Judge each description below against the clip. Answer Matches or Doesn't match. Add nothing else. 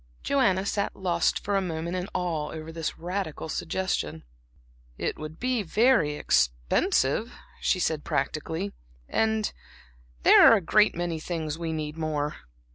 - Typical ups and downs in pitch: Matches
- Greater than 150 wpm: Doesn't match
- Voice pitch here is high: Doesn't match